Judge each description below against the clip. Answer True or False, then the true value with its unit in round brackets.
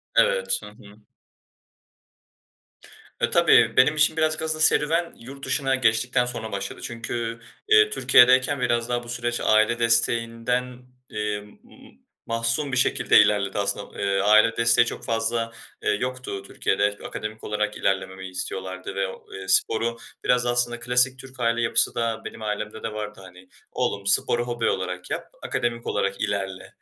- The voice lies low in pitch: True (115 Hz)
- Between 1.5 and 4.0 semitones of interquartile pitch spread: True (3.2 semitones)